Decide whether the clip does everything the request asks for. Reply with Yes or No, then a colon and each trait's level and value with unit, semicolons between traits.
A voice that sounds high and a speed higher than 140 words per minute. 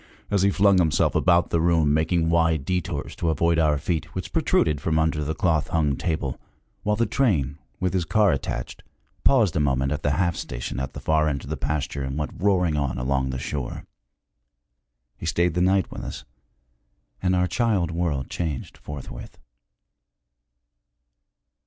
No: very low, 80 Hz; average, 170 wpm